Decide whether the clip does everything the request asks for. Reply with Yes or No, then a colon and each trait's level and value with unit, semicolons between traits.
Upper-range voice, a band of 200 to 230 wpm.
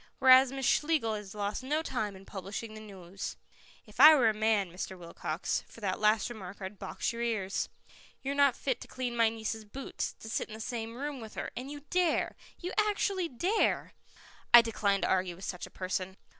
Yes: high, 225 Hz; fast, 205 wpm